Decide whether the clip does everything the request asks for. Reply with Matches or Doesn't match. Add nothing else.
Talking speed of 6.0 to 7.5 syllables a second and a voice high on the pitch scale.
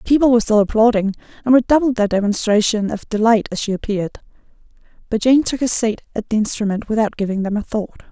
Matches